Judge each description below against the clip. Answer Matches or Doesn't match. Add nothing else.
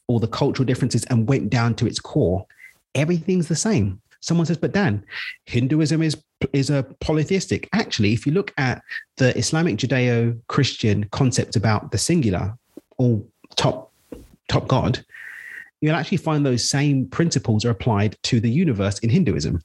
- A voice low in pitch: Matches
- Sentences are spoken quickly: Doesn't match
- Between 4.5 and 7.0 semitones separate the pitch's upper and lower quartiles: Matches